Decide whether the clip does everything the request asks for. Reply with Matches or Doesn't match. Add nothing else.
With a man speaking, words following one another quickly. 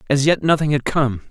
Matches